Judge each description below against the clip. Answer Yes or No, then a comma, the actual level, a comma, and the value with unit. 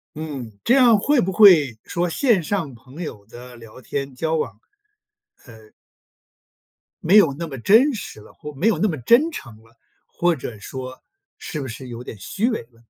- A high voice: No, medium, 150 Hz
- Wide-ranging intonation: Yes, wide, 8.5 semitones